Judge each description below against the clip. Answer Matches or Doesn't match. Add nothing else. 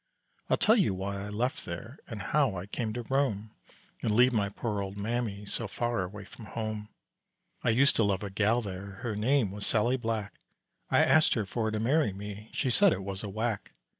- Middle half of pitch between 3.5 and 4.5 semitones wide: Doesn't match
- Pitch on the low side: Matches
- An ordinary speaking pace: Doesn't match